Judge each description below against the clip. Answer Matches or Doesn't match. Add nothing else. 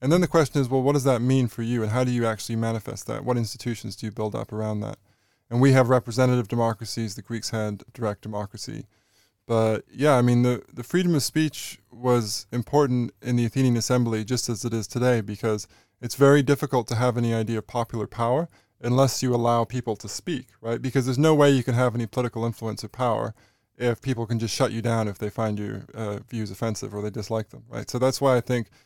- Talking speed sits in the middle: Doesn't match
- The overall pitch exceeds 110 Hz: Matches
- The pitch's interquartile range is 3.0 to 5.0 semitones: Doesn't match